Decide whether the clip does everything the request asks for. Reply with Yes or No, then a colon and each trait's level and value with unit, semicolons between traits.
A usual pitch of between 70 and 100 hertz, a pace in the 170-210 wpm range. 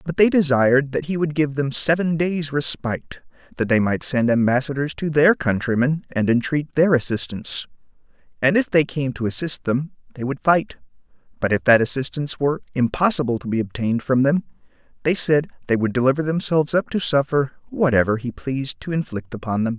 No: low, 135 Hz; average, 180 wpm